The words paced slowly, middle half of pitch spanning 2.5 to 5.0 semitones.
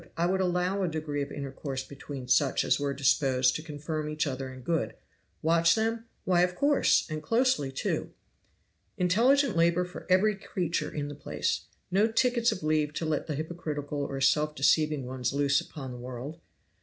No: average, 180 wpm; average, 4.3 semitones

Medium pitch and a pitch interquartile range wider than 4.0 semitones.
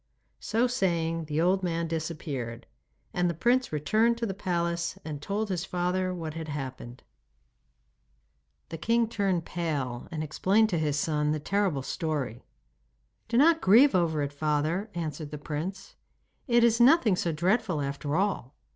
Yes: medium, 170 Hz; average, 4.7 semitones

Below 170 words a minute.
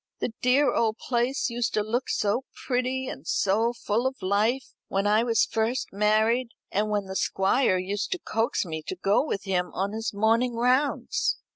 No: average, 180 wpm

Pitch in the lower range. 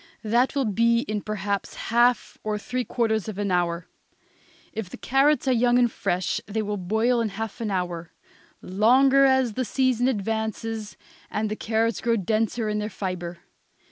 No: high, 220 Hz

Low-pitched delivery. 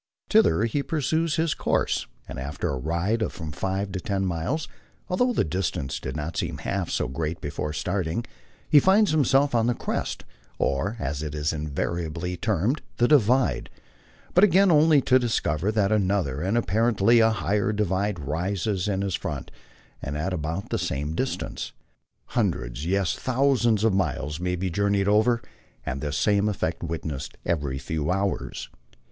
Yes: very low, 95 Hz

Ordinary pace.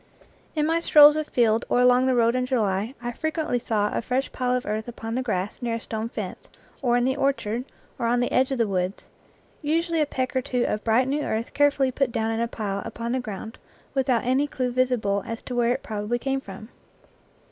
No: fast, 225 wpm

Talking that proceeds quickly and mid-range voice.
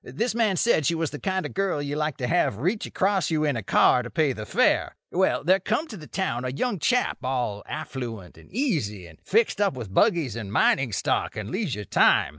Yes: fast, 230 wpm; medium, 150 Hz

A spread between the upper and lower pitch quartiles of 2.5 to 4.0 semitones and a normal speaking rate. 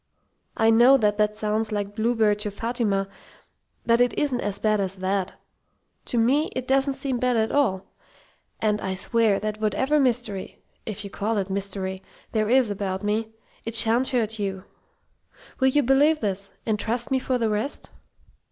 Yes: average, 3.2 semitones; average, 170 wpm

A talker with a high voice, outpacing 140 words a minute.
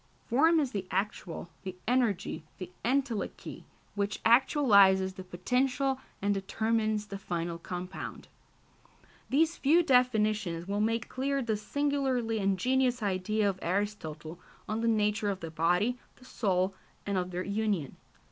No: high, 210 Hz; slow, 135 wpm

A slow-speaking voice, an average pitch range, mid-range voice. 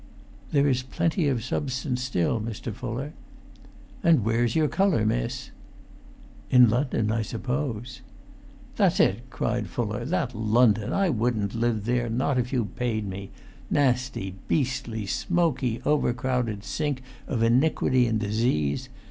No: slow, 130 wpm; average, 3.1 semitones; low, 120 Hz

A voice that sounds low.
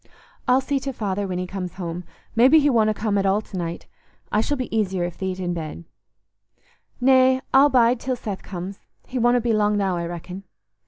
No: high, 205 Hz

